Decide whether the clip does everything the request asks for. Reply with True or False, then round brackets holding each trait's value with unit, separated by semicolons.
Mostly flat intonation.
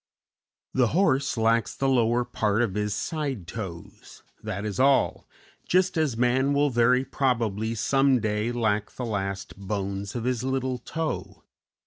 False (4.1 semitones)